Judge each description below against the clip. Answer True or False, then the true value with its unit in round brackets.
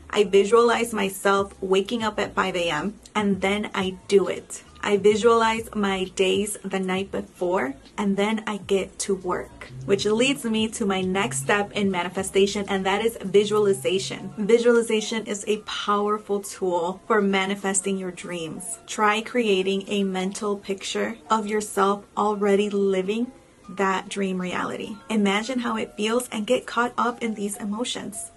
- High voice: True (205 Hz)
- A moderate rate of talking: True (150 wpm)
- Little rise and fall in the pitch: True (2.1 semitones)